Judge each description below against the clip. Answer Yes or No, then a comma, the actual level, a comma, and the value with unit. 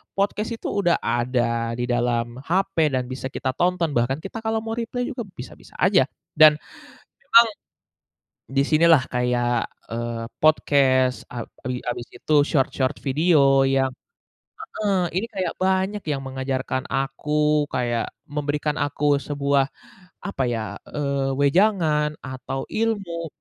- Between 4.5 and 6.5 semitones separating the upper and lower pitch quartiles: Yes, wide, 5.4 semitones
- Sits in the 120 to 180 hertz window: Yes, medium, 140 Hz